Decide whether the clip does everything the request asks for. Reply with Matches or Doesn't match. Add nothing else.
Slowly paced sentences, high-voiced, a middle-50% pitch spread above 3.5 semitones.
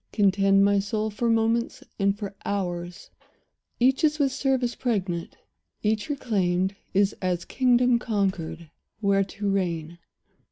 Matches